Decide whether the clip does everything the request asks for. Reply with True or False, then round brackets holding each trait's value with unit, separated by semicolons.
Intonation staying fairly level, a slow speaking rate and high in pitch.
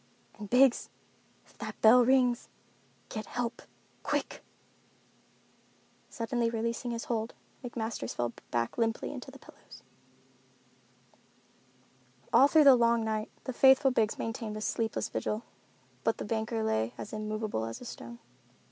True (2.2 semitones; 125 wpm; 225 Hz)